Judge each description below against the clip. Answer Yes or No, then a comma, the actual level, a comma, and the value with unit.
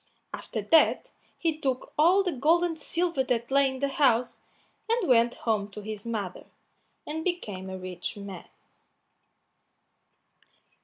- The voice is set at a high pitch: Yes, very high, 260 Hz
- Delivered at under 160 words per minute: Yes, average, 140 wpm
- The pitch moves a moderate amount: No, wide, 7.3 semitones